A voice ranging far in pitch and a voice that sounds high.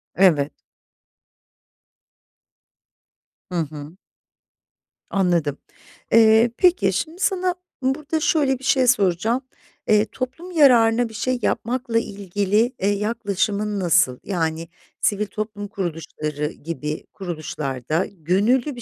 Yes: wide, 6.4 semitones; high, 205 Hz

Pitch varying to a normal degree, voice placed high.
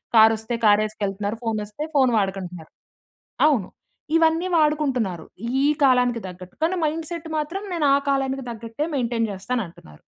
No: wide, 6.5 semitones; high, 235 Hz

